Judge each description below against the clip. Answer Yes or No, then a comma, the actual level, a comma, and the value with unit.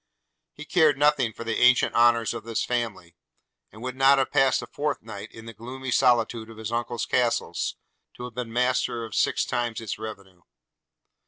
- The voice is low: Yes, low, 120 Hz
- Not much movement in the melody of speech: Yes, narrow, 2.3 semitones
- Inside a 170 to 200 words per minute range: Yes, average, 180 wpm